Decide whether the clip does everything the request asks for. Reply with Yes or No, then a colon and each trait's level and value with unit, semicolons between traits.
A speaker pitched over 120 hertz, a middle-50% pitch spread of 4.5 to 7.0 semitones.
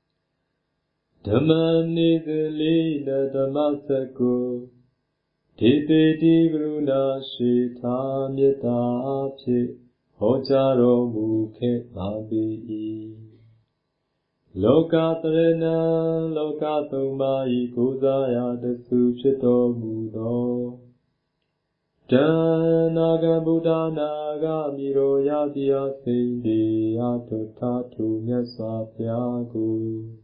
No: low, 135 Hz; average, 4.0 semitones